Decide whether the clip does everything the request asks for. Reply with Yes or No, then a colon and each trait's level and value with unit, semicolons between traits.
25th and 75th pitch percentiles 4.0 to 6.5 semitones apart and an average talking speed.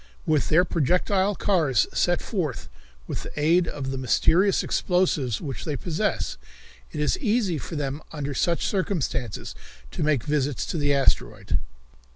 Yes: average, 4.5 semitones; average, 150 wpm